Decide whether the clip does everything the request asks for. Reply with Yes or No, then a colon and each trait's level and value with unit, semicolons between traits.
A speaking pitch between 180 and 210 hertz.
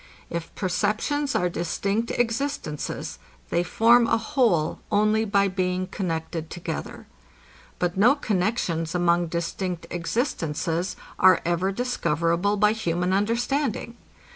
Yes: medium, 185 Hz